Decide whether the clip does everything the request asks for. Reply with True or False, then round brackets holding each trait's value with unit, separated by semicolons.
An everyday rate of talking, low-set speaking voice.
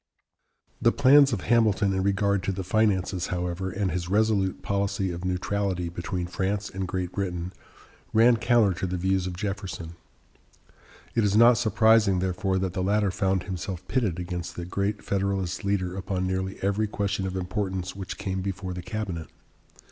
True (165 wpm; 95 Hz)